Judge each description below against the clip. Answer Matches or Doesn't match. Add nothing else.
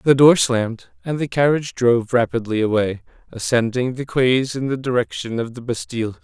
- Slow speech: Doesn't match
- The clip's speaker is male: Matches